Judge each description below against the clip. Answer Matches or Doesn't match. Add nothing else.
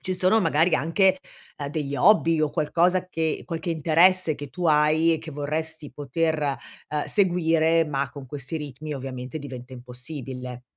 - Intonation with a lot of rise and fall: Doesn't match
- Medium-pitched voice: Matches